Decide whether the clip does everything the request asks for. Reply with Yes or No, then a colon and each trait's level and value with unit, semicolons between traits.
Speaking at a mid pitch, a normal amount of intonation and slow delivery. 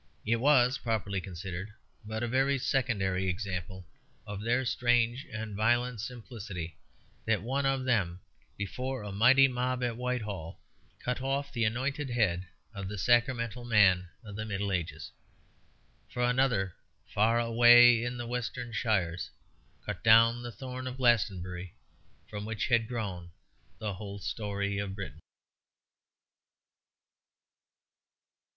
No: low, 115 Hz; average, 3.7 semitones; slow, 130 wpm